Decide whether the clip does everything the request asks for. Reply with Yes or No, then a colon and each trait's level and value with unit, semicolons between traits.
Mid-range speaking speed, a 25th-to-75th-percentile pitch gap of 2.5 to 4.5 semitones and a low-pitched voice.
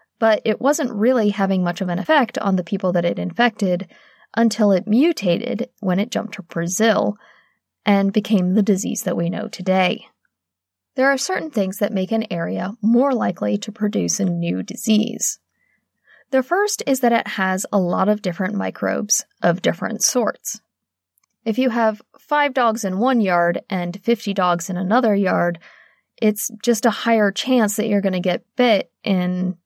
No: average, 175 wpm; average, 3.9 semitones; high, 210 Hz